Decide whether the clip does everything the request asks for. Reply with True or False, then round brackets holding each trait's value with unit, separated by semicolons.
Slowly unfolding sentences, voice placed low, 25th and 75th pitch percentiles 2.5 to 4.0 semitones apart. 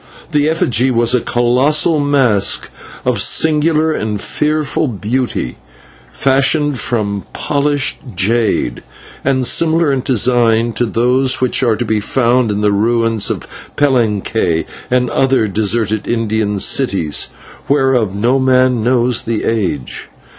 True (125 wpm; 120 Hz; 3.7 semitones)